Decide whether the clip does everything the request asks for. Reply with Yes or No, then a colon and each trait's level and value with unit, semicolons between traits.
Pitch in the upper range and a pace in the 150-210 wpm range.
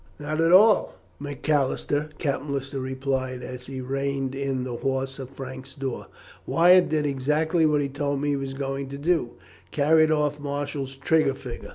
No: medium, 140 Hz; average, 170 wpm